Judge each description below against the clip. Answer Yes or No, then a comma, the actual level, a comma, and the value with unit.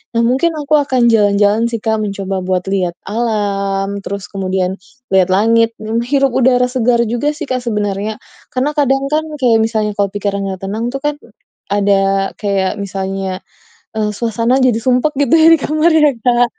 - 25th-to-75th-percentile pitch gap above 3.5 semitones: Yes, average, 4.3 semitones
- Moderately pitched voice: No, high, 220 Hz